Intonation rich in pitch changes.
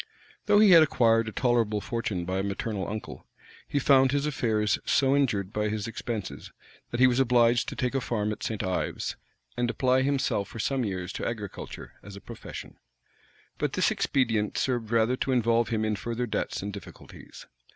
No: average, 3.4 semitones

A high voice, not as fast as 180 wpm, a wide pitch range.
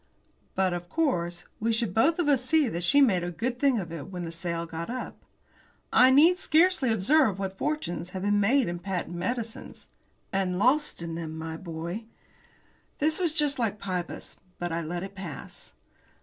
No: high, 195 Hz; average, 185 wpm; wide, 7.1 semitones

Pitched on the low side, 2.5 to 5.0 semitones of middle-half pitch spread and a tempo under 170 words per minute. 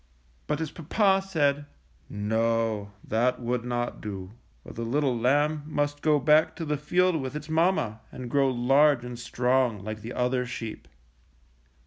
Yes: low, 130 Hz; average, 4.4 semitones; average, 155 wpm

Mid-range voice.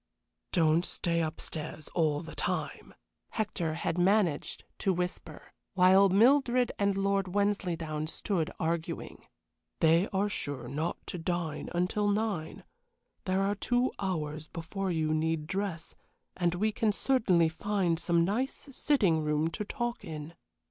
Yes: medium, 180 Hz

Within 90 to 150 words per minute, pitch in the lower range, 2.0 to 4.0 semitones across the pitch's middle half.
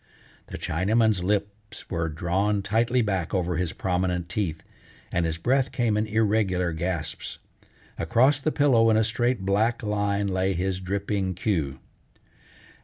Yes: average, 140 wpm; low, 100 Hz; average, 3.5 semitones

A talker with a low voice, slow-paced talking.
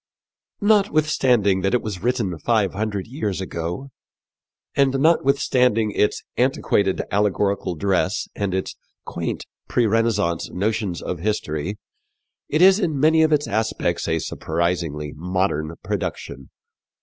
Yes: low, 105 Hz; slow, 120 wpm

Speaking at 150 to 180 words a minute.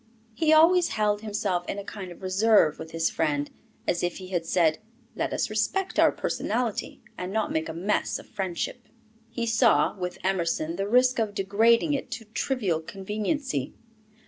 Yes: average, 170 wpm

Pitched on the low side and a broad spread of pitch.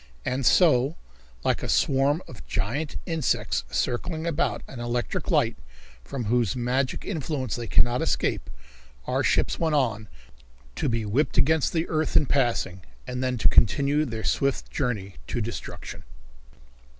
No: low, 130 Hz; average, 4.0 semitones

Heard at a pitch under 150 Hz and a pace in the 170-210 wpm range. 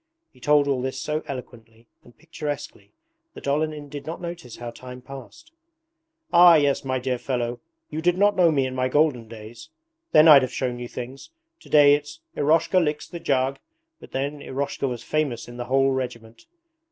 Yes: low, 135 Hz; average, 180 wpm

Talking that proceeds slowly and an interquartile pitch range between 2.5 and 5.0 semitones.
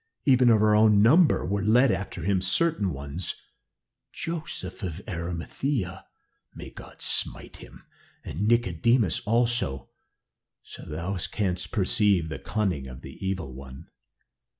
No: slow, 125 wpm; wide, 5.5 semitones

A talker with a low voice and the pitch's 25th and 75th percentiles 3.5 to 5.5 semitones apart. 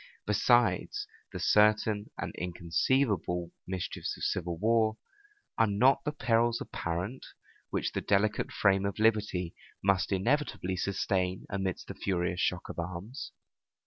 Yes: low, 100 Hz; average, 3.8 semitones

